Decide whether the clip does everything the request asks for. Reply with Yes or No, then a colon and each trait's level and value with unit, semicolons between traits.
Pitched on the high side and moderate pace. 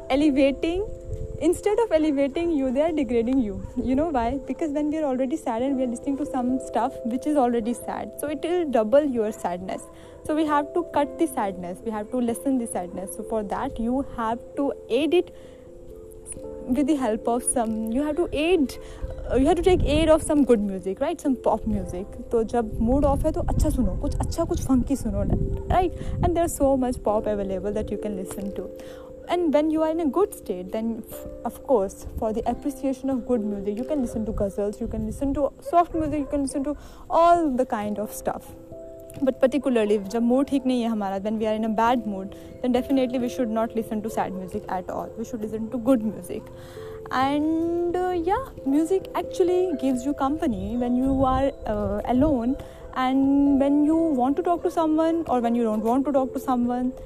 No: very high, 260 Hz; fast, 200 wpm